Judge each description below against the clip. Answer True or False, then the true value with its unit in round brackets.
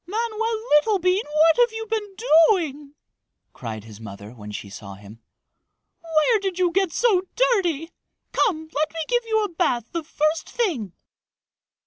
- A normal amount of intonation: False (8.3 semitones)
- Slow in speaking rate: False (150 wpm)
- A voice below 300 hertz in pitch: False (335 Hz)